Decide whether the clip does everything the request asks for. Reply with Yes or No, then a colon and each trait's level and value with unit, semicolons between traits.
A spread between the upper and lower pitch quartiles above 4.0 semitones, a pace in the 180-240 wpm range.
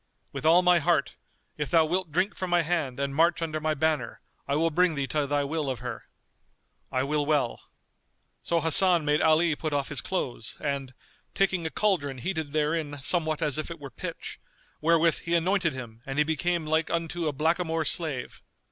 No: average, 2.9 semitones; average, 190 wpm